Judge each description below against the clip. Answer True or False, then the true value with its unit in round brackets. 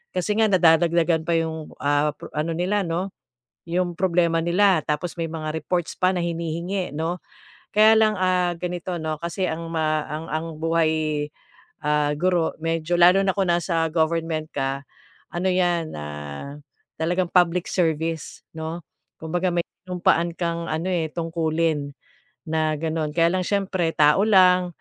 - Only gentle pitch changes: True (2.1 semitones)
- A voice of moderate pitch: True (170 Hz)